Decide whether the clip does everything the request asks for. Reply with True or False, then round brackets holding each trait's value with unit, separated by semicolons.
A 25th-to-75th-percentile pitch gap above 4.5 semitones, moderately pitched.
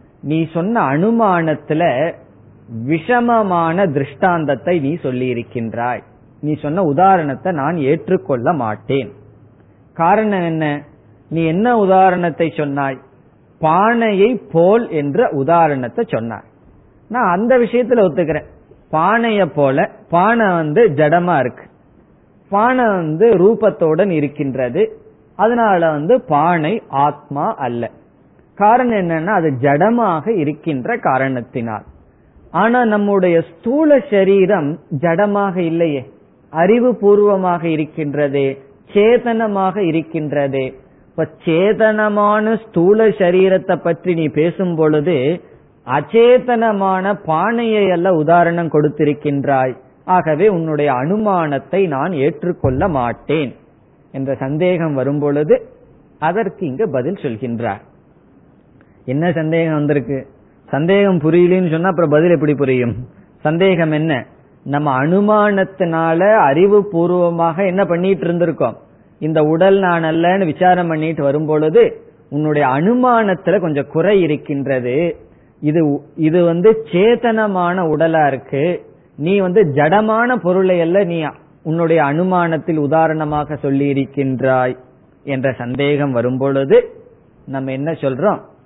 True (5.5 semitones; 165 Hz)